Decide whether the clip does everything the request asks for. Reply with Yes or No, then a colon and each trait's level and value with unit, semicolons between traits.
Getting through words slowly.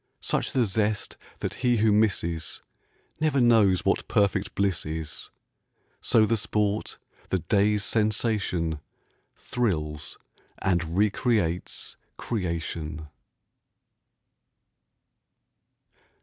Yes: slow, 85 wpm